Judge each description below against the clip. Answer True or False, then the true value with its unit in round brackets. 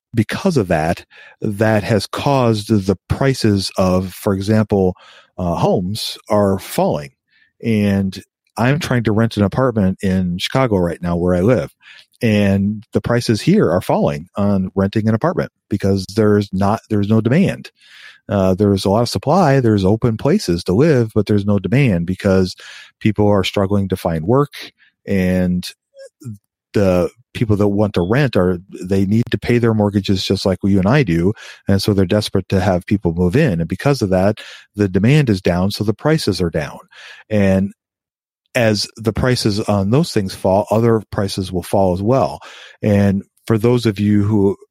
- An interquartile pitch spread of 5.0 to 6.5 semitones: False (2.8 semitones)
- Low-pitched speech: True (105 Hz)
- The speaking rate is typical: True (175 wpm)